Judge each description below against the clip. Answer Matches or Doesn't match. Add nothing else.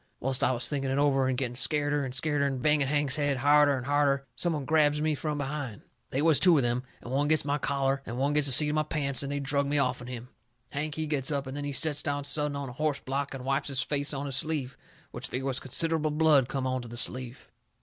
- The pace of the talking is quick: Matches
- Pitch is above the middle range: Doesn't match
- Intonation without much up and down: Matches